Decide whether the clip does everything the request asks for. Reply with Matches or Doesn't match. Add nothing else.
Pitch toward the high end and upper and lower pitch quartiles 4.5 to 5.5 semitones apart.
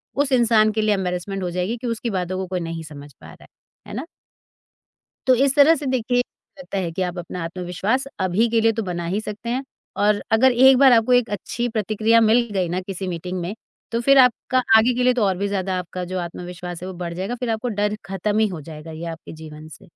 Matches